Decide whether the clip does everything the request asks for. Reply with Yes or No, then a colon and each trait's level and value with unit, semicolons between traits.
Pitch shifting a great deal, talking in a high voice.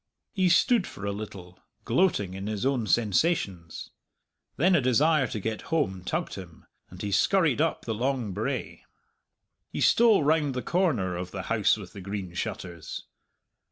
No: wide, 8.4 semitones; low, 110 Hz